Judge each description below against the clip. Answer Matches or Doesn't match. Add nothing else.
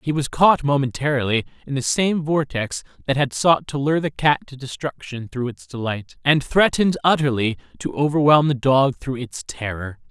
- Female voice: Doesn't match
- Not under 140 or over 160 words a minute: Doesn't match